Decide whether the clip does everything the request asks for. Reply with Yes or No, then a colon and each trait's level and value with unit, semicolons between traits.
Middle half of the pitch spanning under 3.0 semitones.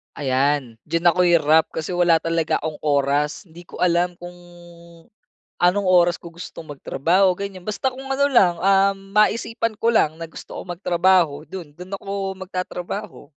No: average, 3.3 semitones